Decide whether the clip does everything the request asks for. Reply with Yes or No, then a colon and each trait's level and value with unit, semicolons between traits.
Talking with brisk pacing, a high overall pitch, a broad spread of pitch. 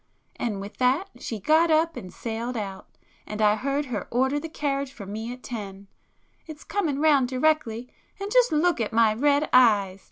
No: average, 180 wpm; very high, 250 Hz; wide, 5.8 semitones